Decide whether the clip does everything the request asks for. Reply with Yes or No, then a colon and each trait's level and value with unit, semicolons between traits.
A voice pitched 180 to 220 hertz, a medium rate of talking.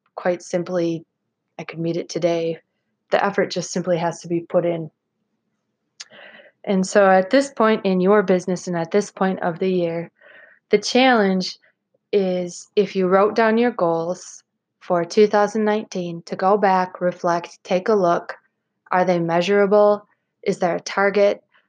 Yes: medium, 185 Hz; average, 155 wpm